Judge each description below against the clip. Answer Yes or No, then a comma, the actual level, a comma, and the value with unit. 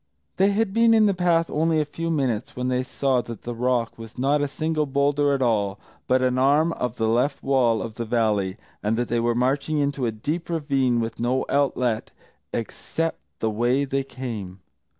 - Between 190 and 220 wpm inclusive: Yes, average, 200 wpm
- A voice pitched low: Yes, low, 130 Hz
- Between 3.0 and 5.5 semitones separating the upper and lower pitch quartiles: Yes, average, 4.0 semitones